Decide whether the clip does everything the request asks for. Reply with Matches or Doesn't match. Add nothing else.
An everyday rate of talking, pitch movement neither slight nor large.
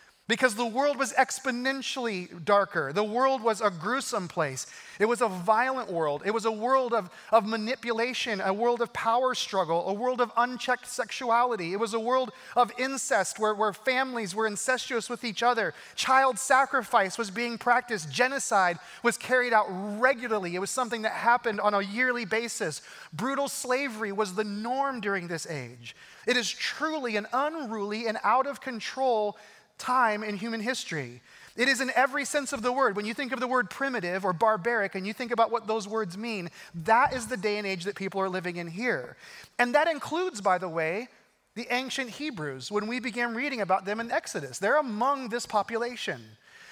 Matches